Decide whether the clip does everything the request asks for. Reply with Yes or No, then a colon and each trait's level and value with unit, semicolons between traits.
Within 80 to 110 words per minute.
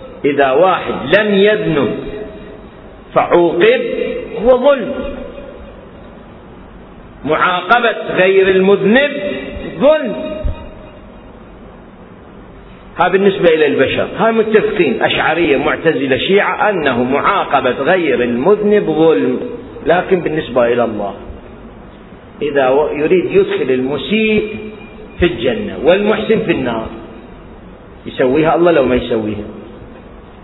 Yes: average, 85 wpm